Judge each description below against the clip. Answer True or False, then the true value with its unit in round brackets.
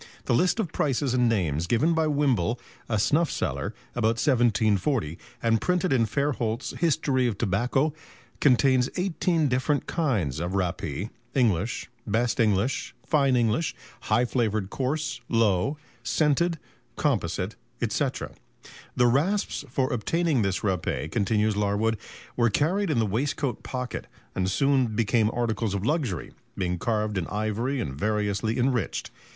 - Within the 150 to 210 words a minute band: False (135 wpm)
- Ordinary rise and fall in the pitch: True (5.0 semitones)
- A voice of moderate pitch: False (120 Hz)